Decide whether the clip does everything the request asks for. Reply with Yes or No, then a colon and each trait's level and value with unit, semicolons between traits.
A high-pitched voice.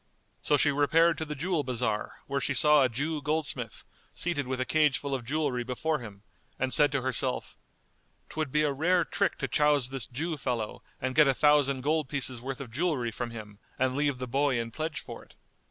No: medium, 140 Hz